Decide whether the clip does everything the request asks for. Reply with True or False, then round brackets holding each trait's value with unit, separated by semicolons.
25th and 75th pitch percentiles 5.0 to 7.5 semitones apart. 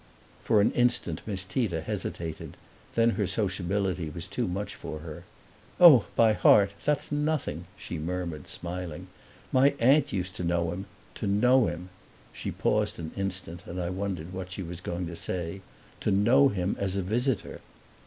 False (4.3 semitones)